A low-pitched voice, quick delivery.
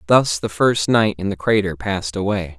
Yes: low, 100 Hz; fast, 210 wpm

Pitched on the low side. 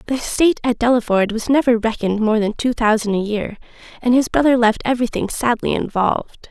No: high, 230 Hz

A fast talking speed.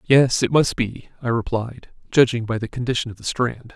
Yes: fast, 210 wpm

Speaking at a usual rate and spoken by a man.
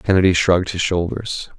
Yes: average, 150 wpm; male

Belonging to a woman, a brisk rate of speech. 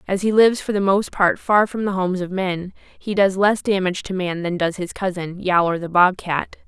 Yes: female; fast, 245 wpm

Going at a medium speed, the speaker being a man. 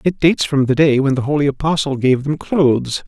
No: fast, 235 wpm; male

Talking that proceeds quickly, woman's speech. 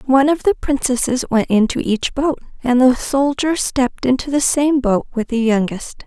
No: average, 190 wpm; female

